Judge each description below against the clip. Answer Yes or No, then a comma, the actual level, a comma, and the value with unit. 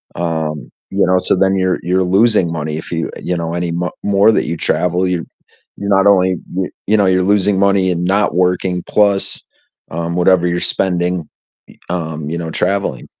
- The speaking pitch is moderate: No, very low, 90 Hz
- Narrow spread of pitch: Yes, narrow, 2.3 semitones